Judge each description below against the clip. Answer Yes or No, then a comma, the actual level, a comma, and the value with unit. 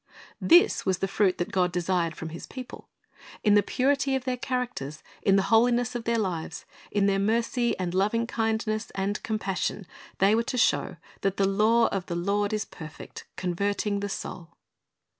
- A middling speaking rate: Yes, average, 180 wpm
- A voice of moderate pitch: No, high, 205 Hz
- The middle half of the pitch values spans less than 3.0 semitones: No, average, 3.7 semitones